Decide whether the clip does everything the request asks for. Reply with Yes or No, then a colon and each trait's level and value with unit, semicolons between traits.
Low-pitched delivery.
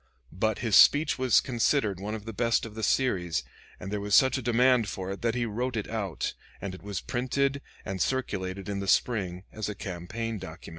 Yes: low, 110 Hz